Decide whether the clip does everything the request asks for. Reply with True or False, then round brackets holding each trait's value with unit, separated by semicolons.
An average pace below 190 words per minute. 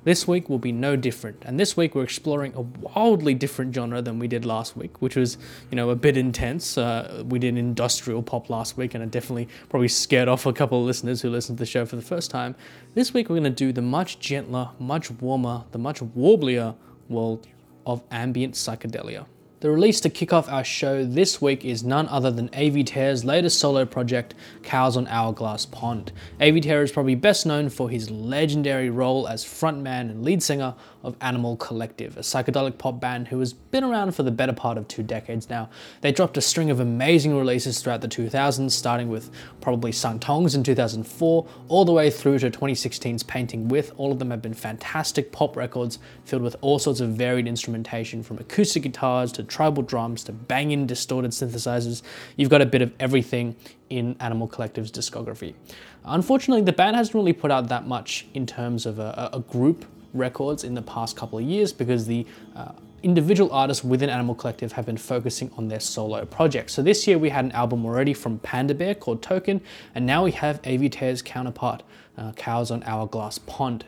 False (205 wpm)